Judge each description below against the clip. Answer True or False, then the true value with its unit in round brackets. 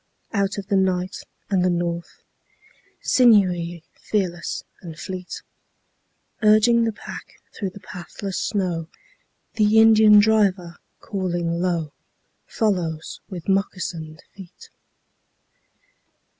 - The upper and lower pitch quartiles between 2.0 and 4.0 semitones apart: True (3.2 semitones)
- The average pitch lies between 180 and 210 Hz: True (185 Hz)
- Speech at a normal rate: False (100 wpm)